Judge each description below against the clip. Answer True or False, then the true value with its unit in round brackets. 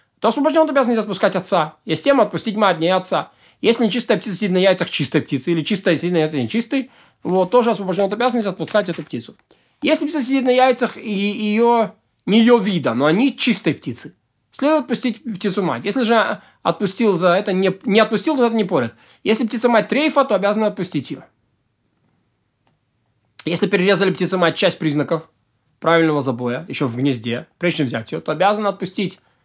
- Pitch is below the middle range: False (200 Hz)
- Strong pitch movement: True (5.9 semitones)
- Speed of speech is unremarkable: False (185 wpm)